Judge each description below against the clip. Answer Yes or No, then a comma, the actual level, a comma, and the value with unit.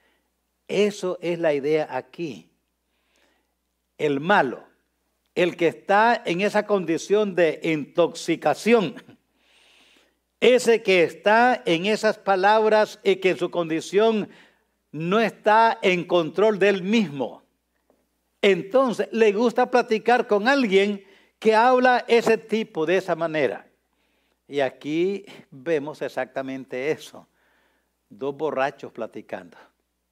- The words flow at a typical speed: No, slow, 105 wpm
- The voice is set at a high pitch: Yes, high, 195 Hz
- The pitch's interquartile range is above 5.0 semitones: Yes, wide, 5.5 semitones